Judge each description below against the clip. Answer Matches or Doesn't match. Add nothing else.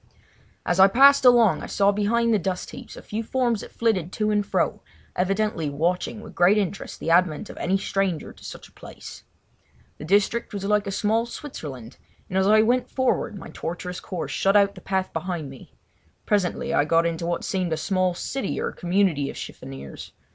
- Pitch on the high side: Matches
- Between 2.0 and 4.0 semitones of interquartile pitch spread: Matches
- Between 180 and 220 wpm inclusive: Matches